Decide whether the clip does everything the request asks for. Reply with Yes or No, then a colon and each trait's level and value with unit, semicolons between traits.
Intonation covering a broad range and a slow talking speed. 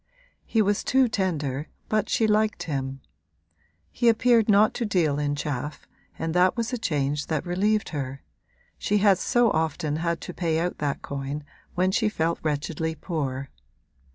No: wide, 6.1 semitones; average, 160 wpm